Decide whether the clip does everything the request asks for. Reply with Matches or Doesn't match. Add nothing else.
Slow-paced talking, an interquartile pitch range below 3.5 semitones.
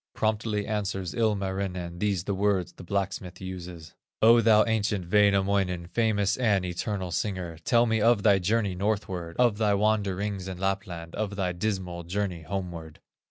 Doesn't match